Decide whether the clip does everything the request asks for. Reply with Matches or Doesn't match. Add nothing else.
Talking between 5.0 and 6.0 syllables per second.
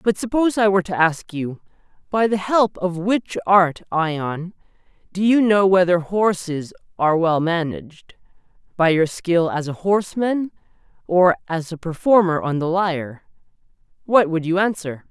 Doesn't match